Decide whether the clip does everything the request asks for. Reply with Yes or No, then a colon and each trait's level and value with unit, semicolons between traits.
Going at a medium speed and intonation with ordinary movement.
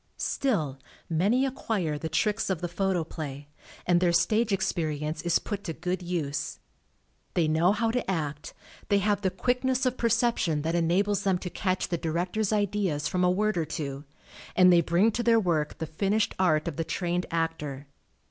Yes: average, 175 wpm; average, 4.4 semitones